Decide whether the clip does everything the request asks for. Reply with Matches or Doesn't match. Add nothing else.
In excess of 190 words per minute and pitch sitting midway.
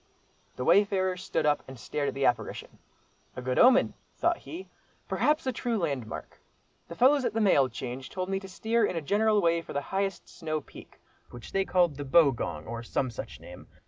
Matches